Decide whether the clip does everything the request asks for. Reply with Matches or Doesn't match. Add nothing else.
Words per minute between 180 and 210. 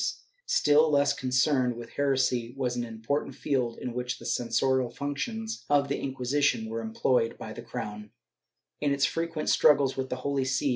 Matches